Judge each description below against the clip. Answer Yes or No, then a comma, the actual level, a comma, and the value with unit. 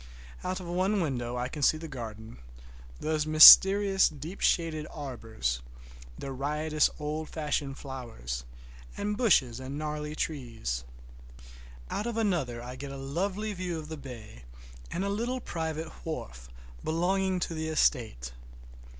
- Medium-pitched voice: Yes, medium, 150 Hz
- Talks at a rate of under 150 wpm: Yes, average, 140 wpm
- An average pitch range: No, wide, 5.7 semitones